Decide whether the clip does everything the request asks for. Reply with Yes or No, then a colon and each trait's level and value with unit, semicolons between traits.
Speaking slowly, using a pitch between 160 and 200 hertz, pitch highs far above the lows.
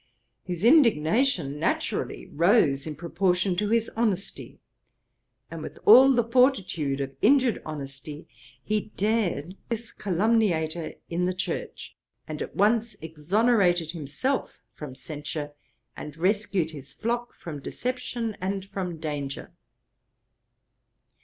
Yes: slow, 115 wpm; medium, 185 Hz; wide, 6.6 semitones